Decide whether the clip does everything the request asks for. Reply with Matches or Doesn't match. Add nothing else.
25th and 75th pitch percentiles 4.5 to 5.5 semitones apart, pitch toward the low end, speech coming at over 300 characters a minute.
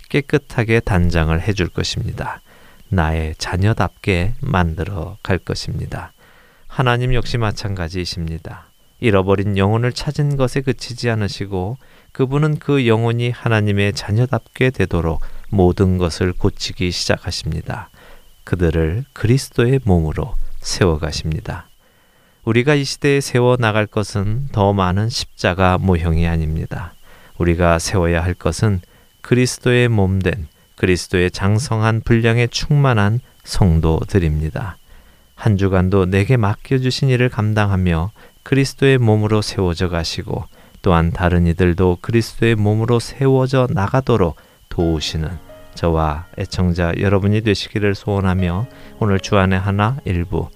Doesn't match